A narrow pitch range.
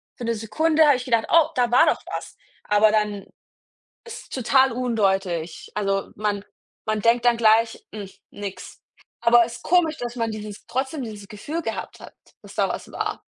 No: average, 3.4 semitones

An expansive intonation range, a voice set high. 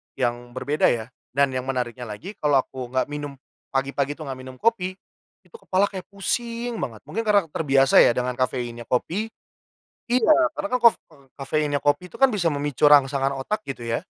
No: wide, 6.3 semitones; medium, 140 Hz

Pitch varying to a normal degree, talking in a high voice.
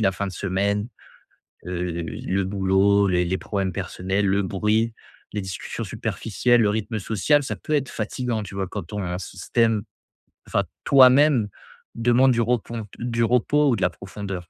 No: average, 3.6 semitones; low, 105 Hz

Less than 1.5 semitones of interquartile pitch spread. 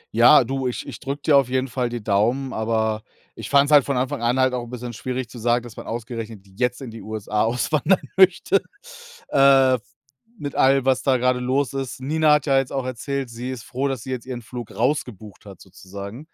No: average, 2.8 semitones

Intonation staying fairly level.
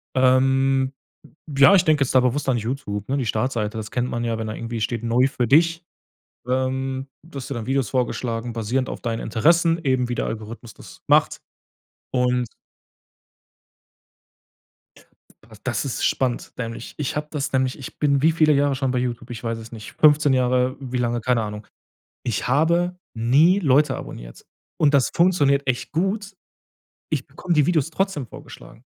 No: average, 3.4 semitones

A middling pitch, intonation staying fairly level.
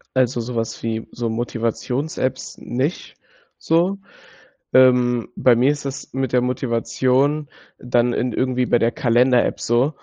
No: low, 125 Hz; narrow, 1.9 semitones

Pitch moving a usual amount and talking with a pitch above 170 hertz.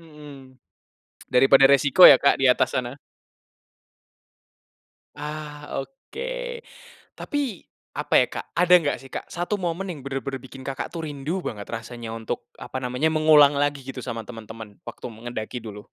No: average, 3.9 semitones; low, 135 Hz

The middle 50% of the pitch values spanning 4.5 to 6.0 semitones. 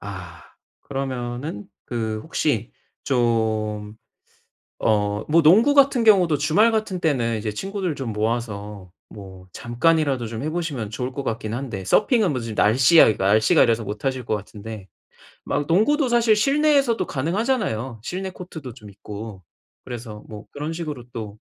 No: wide, 7.7 semitones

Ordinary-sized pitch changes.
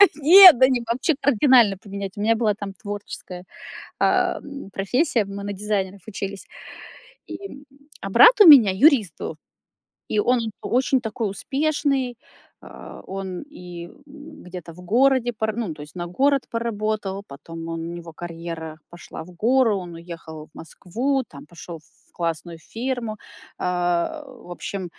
No: wide, 6.6 semitones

